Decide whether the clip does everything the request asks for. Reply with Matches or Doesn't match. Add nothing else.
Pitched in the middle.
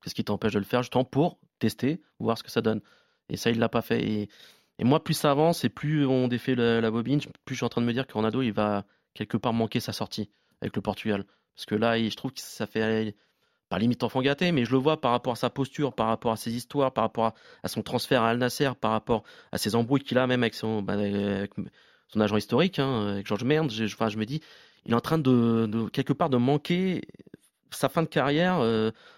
Doesn't match